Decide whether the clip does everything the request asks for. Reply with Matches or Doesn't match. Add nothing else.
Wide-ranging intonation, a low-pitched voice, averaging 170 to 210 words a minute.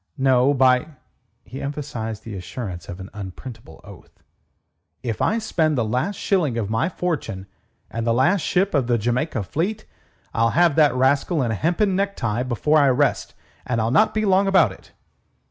Matches